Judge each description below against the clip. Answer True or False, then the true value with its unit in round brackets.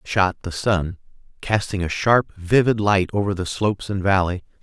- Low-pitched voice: True (95 Hz)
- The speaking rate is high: False (180 wpm)